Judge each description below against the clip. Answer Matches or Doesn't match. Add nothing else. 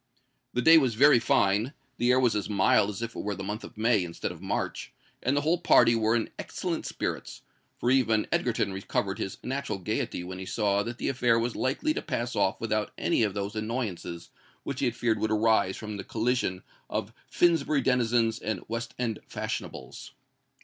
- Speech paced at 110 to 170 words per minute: Doesn't match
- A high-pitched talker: Doesn't match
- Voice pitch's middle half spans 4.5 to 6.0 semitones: Doesn't match